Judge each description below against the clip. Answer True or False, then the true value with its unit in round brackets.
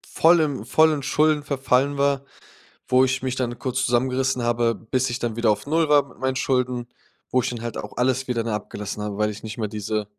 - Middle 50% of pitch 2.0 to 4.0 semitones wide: True (2.6 semitones)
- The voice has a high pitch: False (125 Hz)